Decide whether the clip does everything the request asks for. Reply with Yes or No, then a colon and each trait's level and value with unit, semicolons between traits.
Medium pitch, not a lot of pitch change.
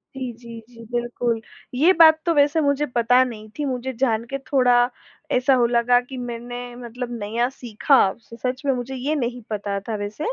No: high, 245 Hz; narrow, 2.2 semitones